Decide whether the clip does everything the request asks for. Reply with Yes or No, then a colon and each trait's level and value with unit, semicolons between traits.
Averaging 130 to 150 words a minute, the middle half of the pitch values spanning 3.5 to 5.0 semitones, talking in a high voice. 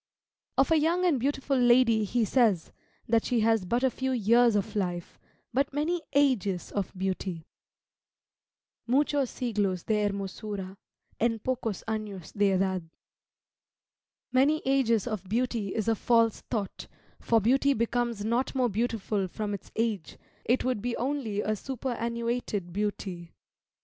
Yes: average, 140 wpm; average, 4.0 semitones; high, 225 Hz